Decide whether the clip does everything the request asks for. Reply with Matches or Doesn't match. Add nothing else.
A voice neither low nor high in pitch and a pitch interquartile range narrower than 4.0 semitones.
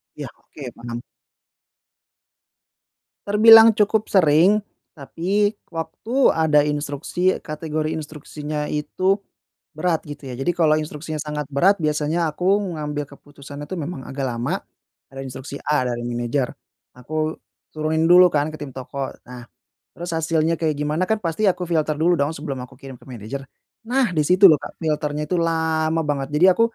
Matches